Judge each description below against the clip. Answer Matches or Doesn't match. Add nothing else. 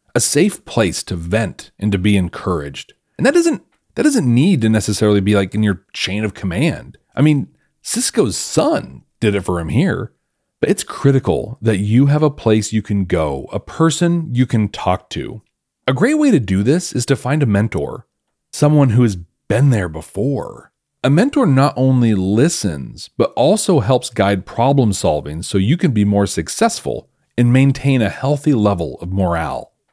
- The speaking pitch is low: Matches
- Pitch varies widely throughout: Matches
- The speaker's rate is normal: Matches